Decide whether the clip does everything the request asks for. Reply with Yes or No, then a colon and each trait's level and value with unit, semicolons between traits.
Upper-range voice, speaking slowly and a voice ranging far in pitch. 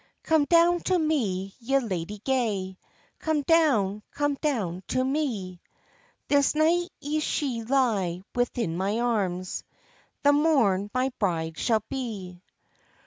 Yes: high, 240 Hz; slow, 125 wpm; wide, 7.2 semitones